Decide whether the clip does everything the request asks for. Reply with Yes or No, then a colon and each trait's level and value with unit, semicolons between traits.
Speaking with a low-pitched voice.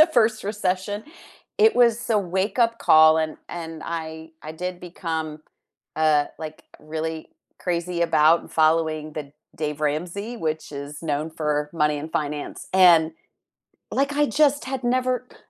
No: medium, 160 Hz